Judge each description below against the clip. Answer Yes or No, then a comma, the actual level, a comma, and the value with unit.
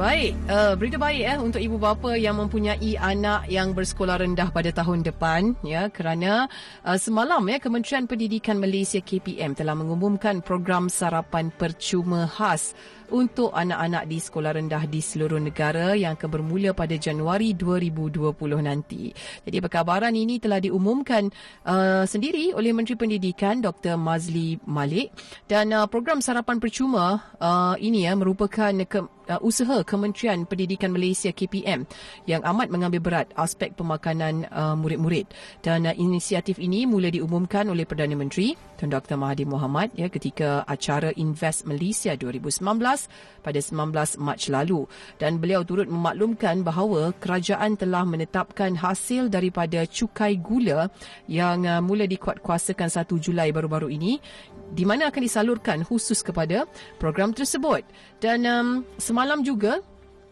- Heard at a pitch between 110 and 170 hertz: No, medium, 185 Hz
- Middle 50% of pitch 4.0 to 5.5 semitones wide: Yes, average, 4.4 semitones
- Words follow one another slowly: No, average, 135 wpm